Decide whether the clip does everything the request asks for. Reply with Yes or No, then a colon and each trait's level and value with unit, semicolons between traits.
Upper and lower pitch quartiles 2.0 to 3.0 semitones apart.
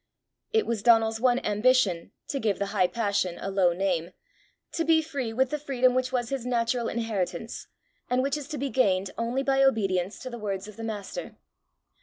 No: average, 4.6 semitones